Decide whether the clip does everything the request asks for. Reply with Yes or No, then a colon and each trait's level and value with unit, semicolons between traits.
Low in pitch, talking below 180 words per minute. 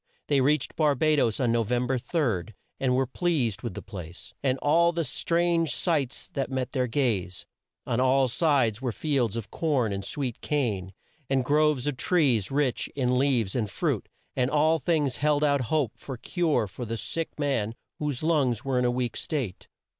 No: low, 130 Hz; average, 190 wpm